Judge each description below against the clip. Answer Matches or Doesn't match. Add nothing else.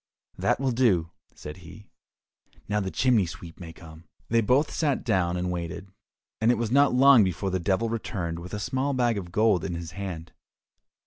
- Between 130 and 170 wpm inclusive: Doesn't match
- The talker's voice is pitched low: Matches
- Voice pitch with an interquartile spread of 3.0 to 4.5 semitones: Doesn't match